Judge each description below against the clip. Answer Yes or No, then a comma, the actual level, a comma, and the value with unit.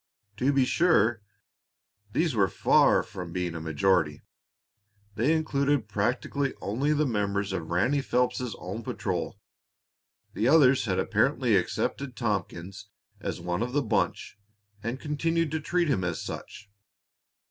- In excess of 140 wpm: No, slow, 135 wpm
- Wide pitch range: Yes, wide, 6.7 semitones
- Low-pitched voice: Yes, low, 115 Hz